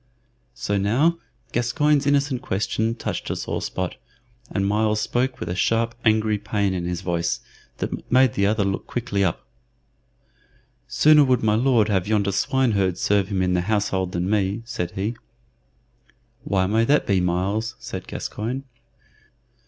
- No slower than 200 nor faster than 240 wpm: No, average, 150 wpm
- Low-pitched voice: Yes, low, 105 Hz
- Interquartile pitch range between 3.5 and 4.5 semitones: Yes, average, 3.9 semitones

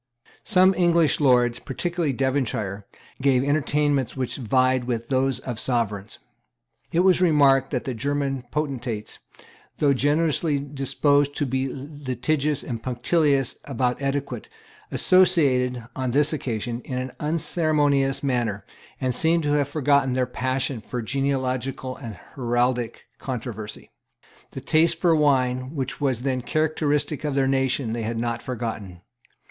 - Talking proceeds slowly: Yes, slow, 130 wpm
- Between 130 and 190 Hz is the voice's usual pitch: Yes, low, 135 Hz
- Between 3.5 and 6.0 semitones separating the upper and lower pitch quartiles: No, average, 2.8 semitones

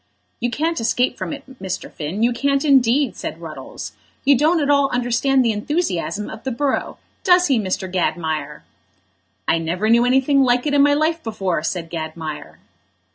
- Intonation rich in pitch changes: Yes, wide, 7.0 semitones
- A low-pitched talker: No, high, 245 Hz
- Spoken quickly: No, average, 175 wpm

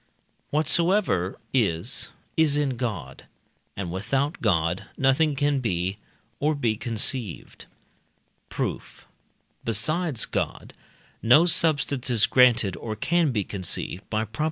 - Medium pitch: No, low, 120 Hz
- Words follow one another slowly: Yes, slow, 110 wpm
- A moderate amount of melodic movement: No, wide, 6.1 semitones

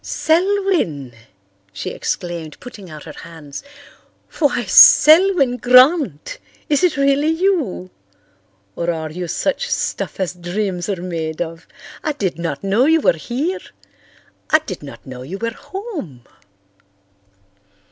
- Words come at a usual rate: No, slow, 125 wpm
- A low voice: No, high, 200 Hz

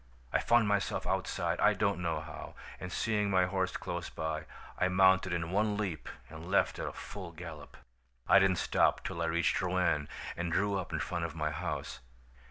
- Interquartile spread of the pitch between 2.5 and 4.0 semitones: Yes, average, 3.1 semitones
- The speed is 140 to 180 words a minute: No, average, 190 wpm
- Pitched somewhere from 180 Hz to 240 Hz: No, very low, 90 Hz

